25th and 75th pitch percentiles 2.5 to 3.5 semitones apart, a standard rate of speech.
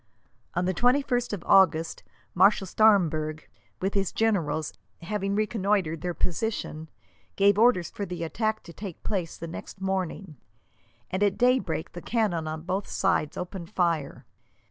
No: average, 3.9 semitones; average, 145 wpm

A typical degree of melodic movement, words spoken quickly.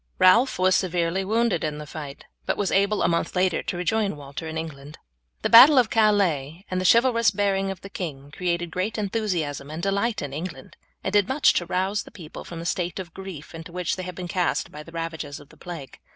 Yes: average, 3.8 semitones; fast, 225 wpm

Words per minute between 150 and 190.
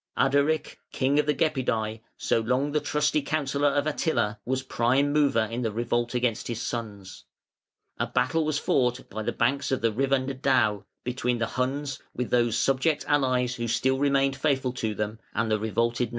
Yes: average, 180 wpm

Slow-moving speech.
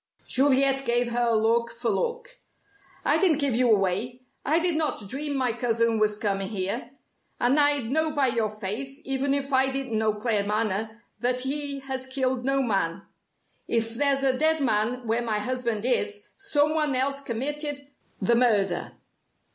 No: average, 160 wpm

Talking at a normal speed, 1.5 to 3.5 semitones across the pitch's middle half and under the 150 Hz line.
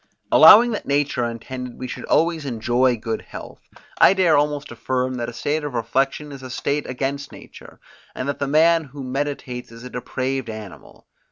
Yes: average, 180 wpm; average, 2.9 semitones; low, 135 Hz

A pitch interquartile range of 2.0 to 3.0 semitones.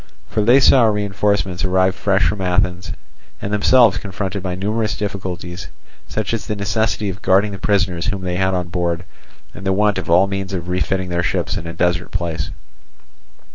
Yes: narrow, 2.4 semitones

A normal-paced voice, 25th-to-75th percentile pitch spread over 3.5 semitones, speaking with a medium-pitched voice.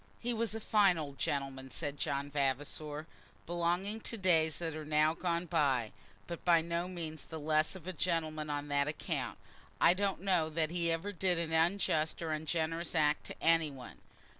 No: average, 185 wpm; narrow, 2.5 semitones; medium, 160 Hz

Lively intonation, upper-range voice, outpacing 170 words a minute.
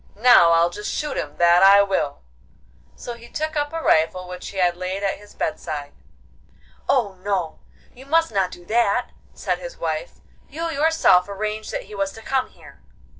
Yes: wide, 5.9 semitones; high, 200 Hz; average, 180 wpm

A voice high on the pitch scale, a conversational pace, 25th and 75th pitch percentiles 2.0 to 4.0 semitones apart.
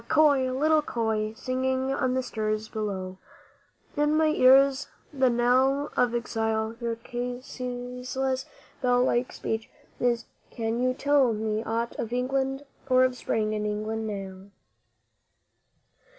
No: high, 245 Hz; slow, 125 wpm; average, 3.0 semitones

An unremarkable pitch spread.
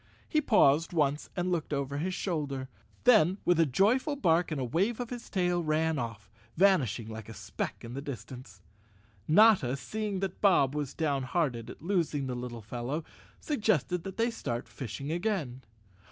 No: wide, 6.7 semitones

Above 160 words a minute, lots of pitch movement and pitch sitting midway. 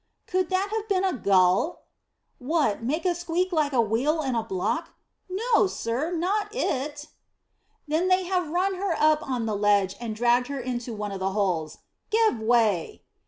No: average, 175 wpm; wide, 8.4 semitones; very high, 290 Hz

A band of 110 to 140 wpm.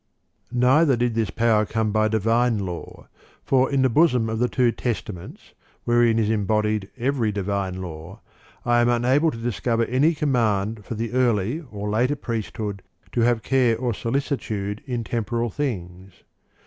No: average, 160 wpm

